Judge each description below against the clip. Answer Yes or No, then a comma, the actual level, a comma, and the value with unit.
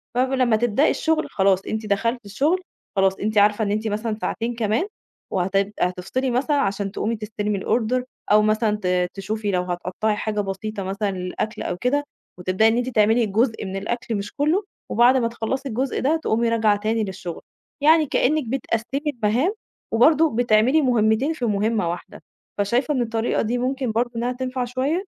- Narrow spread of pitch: No, average, 3.5 semitones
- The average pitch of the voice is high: Yes, high, 225 Hz